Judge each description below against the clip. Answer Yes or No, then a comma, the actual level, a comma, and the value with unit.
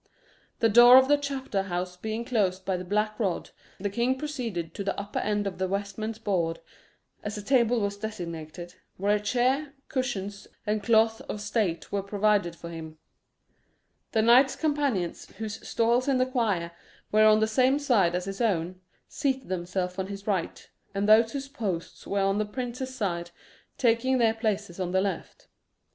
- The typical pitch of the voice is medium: No, high, 210 Hz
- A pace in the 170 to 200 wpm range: Yes, average, 175 wpm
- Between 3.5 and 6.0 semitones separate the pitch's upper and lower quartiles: Yes, average, 4.1 semitones